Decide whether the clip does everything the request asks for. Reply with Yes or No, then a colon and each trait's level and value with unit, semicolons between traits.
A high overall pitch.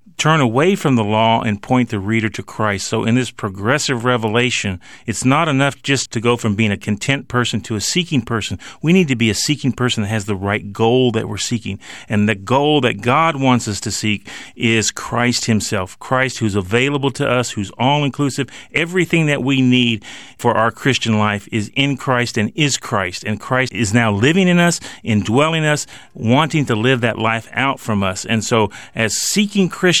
No: low, 120 Hz